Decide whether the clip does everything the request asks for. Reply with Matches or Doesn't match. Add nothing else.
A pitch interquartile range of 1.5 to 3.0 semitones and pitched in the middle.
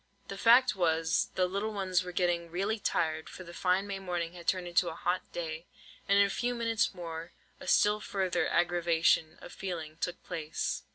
Matches